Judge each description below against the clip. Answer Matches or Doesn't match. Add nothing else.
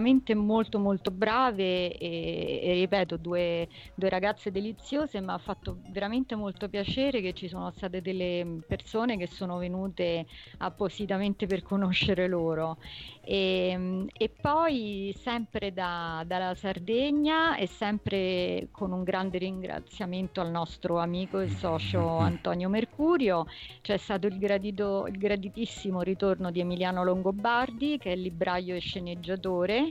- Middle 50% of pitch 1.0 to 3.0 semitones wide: Matches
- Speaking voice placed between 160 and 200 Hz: Matches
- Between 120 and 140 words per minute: Matches